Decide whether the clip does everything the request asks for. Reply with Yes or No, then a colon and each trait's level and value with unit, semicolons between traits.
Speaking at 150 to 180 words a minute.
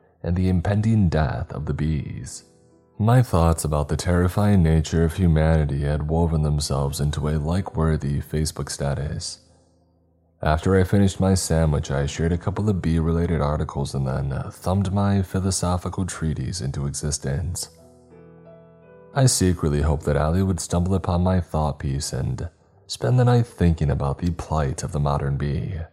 Yes: average, 155 wpm